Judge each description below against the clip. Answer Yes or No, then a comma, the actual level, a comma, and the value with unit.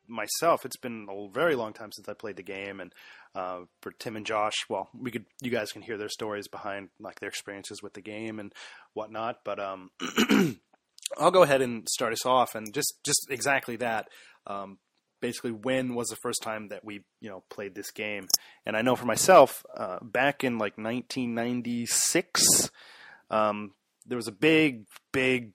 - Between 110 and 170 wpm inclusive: No, average, 190 wpm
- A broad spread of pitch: No, average, 3.2 semitones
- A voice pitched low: Yes, low, 110 Hz